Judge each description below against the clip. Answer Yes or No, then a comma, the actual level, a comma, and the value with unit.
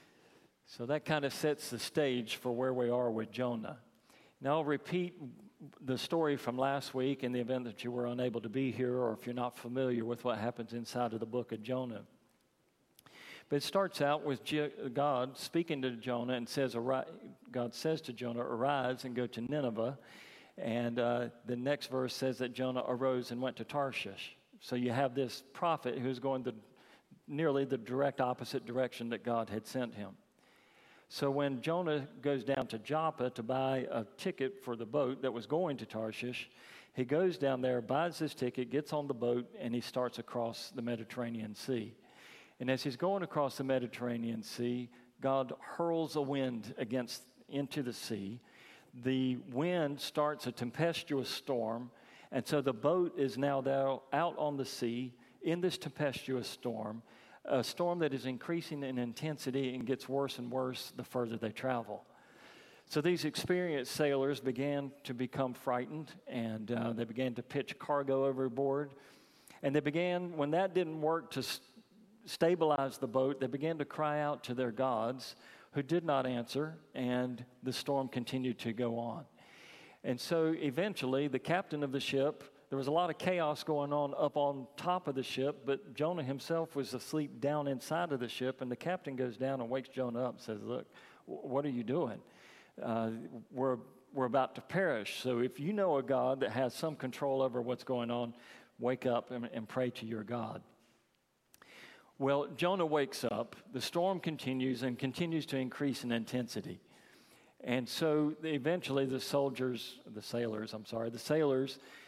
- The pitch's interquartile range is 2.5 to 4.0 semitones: Yes, average, 3.0 semitones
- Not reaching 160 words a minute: No, average, 180 wpm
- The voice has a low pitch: Yes, low, 130 Hz